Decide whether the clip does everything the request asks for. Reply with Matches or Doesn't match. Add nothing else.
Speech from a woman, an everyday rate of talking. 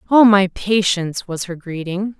Matches